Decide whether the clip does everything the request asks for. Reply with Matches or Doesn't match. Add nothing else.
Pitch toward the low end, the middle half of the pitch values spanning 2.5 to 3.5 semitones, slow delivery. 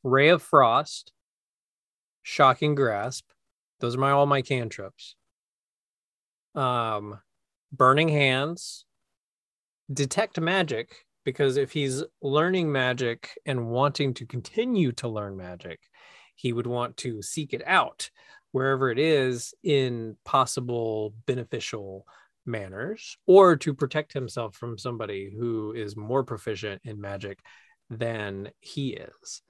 Doesn't match